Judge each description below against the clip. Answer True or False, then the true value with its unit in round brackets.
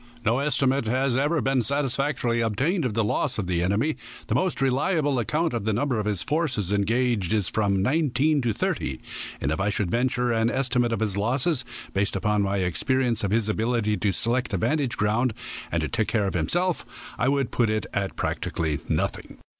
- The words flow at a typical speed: True (195 wpm)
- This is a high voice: False (120 Hz)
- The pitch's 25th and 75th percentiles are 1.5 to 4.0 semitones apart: False (4.7 semitones)